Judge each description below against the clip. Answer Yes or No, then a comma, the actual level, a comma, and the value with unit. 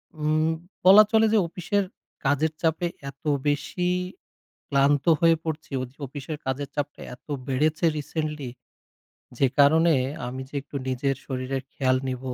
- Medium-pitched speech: Yes, medium, 145 Hz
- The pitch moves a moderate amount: Yes, average, 3.1 semitones